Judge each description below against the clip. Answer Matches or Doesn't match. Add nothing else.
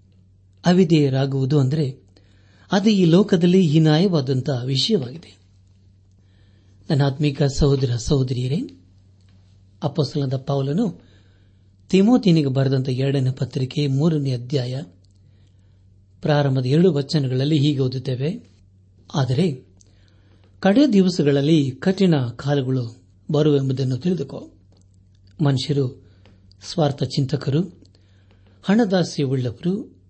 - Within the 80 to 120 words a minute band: Doesn't match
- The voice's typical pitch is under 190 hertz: Matches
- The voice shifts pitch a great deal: Matches